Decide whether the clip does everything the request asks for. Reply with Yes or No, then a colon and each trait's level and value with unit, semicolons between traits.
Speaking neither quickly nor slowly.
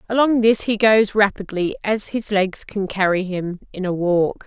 Yes: average, 175 wpm